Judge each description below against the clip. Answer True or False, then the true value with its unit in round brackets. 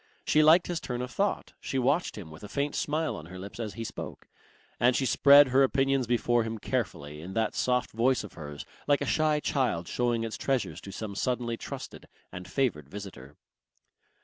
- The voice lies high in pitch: False (120 Hz)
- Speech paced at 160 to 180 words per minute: False (200 wpm)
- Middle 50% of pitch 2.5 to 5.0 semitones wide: False (5.5 semitones)